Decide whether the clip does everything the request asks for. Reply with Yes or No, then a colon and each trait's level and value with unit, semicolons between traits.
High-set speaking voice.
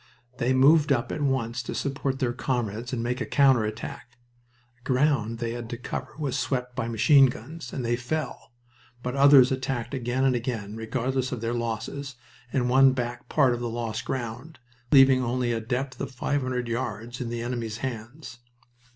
No: low, 125 Hz